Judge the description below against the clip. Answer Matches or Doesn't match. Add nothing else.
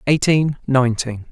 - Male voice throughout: Matches